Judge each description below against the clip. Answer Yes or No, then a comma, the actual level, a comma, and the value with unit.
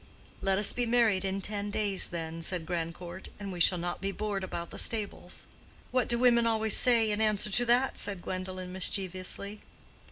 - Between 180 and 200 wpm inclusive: Yes, average, 185 wpm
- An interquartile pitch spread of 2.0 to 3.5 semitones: Yes, average, 3.0 semitones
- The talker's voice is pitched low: No, high, 195 Hz